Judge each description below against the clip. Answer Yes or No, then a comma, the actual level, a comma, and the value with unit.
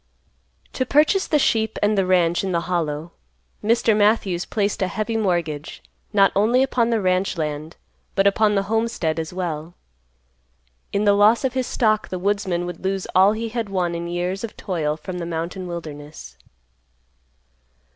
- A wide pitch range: No, average, 3.9 semitones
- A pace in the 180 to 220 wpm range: No, average, 165 wpm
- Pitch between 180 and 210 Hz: Yes, high, 190 Hz